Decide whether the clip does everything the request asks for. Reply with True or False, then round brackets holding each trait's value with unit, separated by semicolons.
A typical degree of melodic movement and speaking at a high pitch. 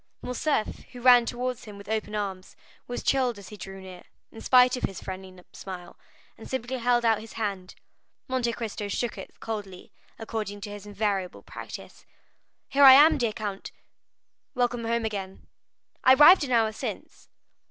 True (3.6 semitones; 220 Hz)